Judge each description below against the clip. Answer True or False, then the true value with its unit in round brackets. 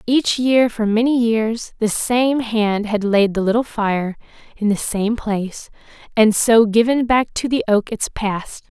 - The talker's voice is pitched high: True (220 Hz)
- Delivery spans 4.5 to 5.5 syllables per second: False (4.0 syllables/s)